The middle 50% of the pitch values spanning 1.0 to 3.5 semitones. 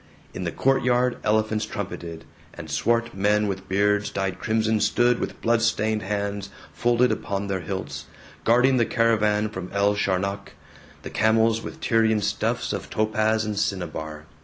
Yes: narrow, 2.5 semitones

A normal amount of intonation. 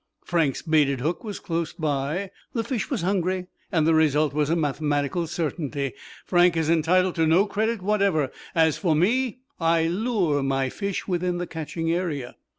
Yes: average, 3.4 semitones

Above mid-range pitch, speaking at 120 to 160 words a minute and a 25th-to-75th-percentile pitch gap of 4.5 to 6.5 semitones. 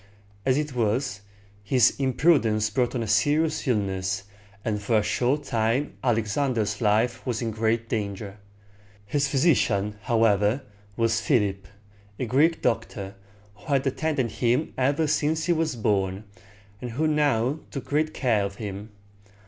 No: low, 115 Hz; average, 140 wpm; average, 4.9 semitones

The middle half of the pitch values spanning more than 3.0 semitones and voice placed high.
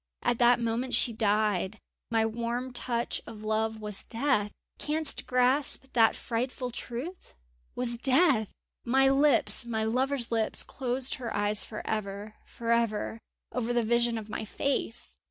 No: narrow, 2.5 semitones; high, 235 Hz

